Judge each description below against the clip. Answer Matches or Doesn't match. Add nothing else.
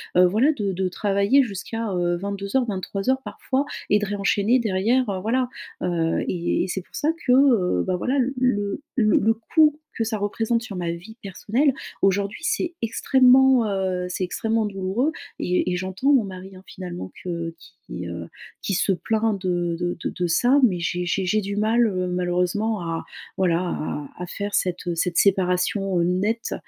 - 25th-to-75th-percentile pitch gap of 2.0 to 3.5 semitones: Doesn't match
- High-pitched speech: Matches